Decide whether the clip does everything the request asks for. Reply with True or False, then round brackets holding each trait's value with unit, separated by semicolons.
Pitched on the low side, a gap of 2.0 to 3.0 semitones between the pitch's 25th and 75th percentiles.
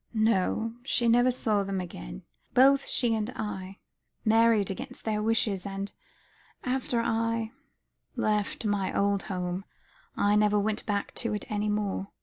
False (210 Hz; 2.4 semitones)